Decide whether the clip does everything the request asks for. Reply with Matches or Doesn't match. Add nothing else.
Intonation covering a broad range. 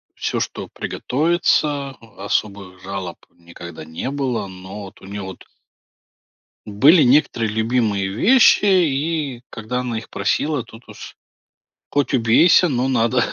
Matches